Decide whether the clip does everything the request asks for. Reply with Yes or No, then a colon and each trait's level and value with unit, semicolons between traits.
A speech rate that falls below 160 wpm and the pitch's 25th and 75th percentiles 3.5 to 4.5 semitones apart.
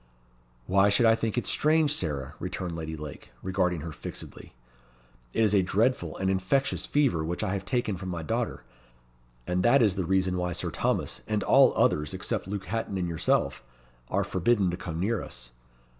No: average, 185 wpm; average, 4.0 semitones